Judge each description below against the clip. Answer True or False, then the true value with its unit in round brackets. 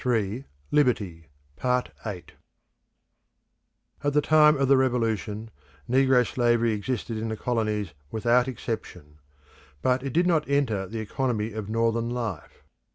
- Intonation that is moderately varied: True (3.3 semitones)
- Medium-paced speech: False (125 wpm)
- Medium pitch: False (115 Hz)